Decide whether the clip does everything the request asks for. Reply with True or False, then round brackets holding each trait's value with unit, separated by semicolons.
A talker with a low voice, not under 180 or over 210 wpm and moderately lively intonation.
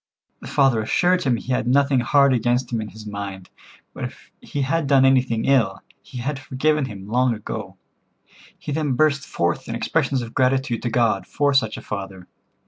True (125 Hz; 190 wpm; 4.0 semitones)